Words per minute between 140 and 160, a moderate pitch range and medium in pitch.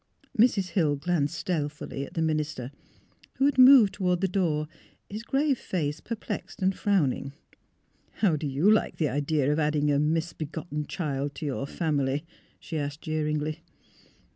No: average, 170 wpm; average, 4.1 semitones; medium, 155 Hz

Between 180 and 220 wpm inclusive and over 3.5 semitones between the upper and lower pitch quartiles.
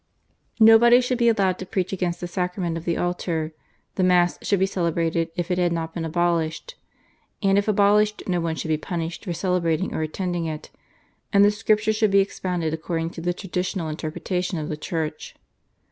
No: average, 190 wpm; average, 3.0 semitones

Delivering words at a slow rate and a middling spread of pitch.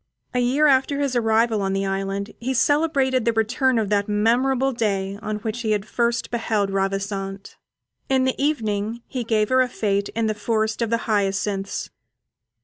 No: average, 170 wpm; average, 3.8 semitones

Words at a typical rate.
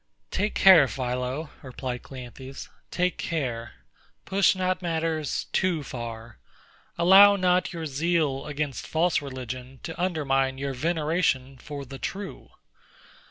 No: slow, 115 wpm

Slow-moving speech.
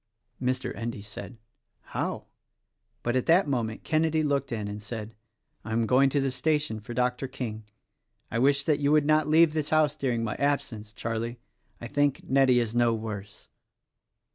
No: average, 170 wpm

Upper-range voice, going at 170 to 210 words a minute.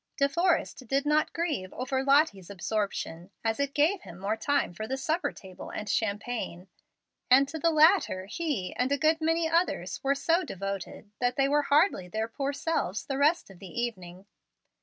Yes: very high, 270 Hz; average, 180 wpm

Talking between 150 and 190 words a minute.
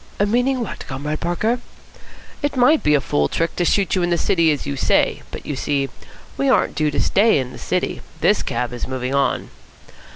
No: fast, 205 wpm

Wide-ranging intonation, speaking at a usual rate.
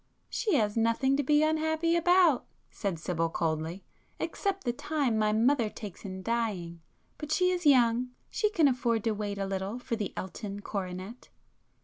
Yes: wide, 7.0 semitones; average, 160 wpm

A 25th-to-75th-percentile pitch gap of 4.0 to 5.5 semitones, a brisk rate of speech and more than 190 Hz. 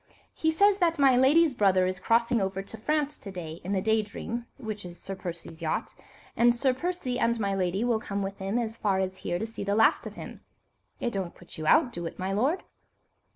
Yes: average, 4.6 semitones; fast, 230 wpm; high, 215 Hz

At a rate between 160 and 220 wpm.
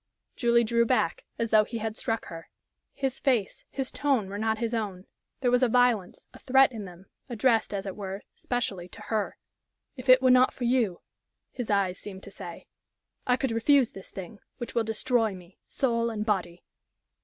Yes: average, 190 wpm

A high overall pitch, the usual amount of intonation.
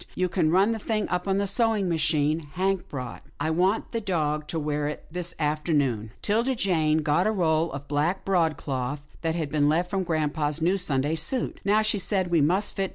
No: medium, 160 Hz; average, 4.2 semitones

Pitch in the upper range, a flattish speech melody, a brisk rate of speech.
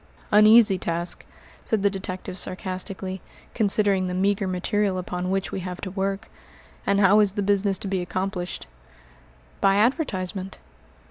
No: high, 195 Hz; narrow, 1.6 semitones; average, 145 wpm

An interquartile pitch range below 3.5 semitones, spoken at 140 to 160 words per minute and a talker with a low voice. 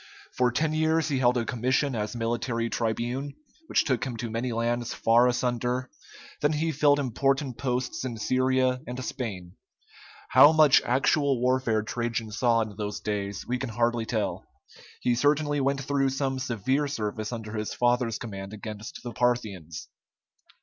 Yes: average, 2.7 semitones; average, 155 wpm; low, 125 Hz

